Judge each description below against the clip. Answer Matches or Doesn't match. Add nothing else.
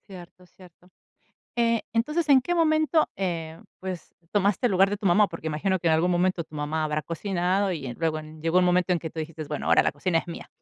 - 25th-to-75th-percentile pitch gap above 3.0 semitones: Matches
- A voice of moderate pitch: Matches